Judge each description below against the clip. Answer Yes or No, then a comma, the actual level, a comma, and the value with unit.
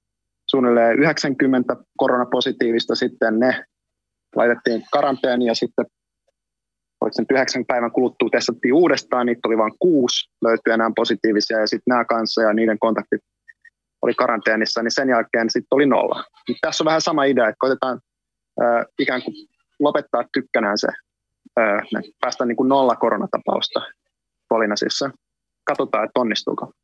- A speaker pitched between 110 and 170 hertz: Yes, low, 120 Hz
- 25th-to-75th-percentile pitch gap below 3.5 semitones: Yes, average, 2.9 semitones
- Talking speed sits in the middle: Yes, average, 135 wpm